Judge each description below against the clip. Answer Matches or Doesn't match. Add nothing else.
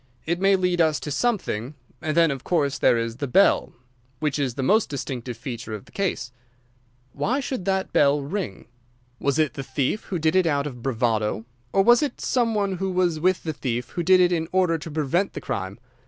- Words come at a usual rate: Doesn't match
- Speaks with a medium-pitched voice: Matches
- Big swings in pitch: Matches